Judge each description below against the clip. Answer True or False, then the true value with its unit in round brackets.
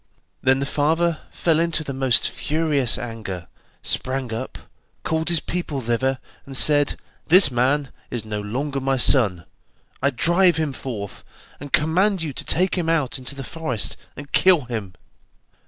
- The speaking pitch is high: False (140 Hz)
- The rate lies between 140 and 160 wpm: True (155 wpm)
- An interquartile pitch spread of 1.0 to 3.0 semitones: False (4.5 semitones)